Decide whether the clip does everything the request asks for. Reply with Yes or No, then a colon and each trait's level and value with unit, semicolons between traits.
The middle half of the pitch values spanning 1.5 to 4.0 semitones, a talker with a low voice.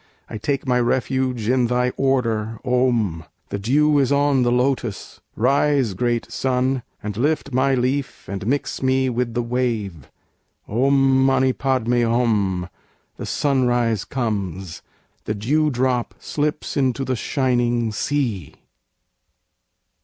Yes: average, 2.7 semitones; low, 125 Hz